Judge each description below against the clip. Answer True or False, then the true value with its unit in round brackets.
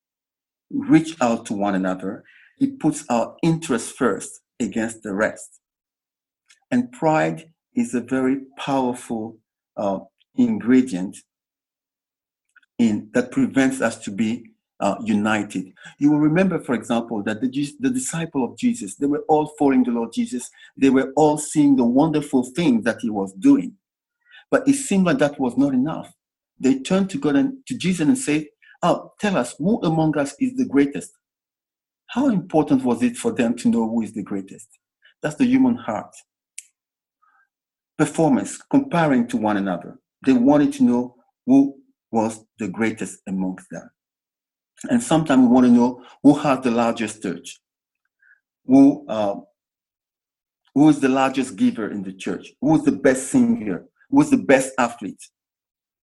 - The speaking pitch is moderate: True (155 Hz)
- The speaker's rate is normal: True (155 wpm)